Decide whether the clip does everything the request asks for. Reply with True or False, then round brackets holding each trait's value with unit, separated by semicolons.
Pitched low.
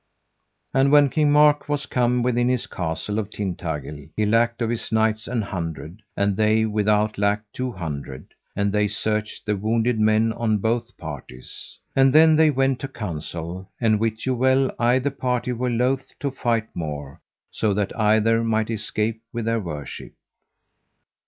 True (110 Hz)